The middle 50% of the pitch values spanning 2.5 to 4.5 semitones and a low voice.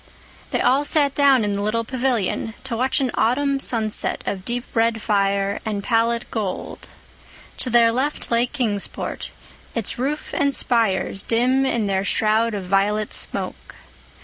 No: average, 3.7 semitones; high, 230 Hz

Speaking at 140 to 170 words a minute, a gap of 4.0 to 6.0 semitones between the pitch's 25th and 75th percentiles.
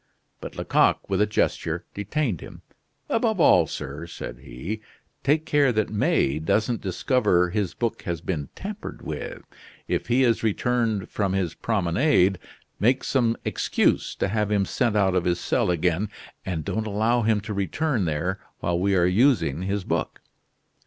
Yes: average, 160 wpm; average, 4.6 semitones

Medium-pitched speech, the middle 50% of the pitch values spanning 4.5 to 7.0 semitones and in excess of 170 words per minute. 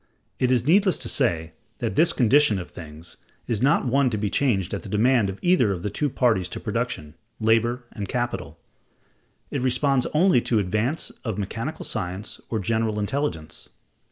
No: low, 115 Hz; average, 5.0 semitones; average, 180 wpm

